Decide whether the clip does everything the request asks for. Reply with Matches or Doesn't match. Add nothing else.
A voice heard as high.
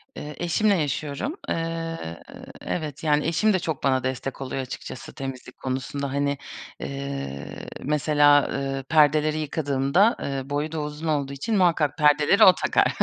Doesn't match